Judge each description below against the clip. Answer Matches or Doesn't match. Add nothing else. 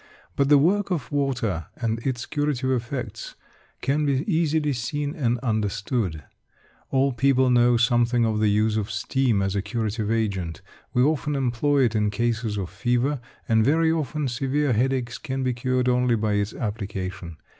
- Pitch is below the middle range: Matches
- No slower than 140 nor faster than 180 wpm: Matches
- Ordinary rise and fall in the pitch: Matches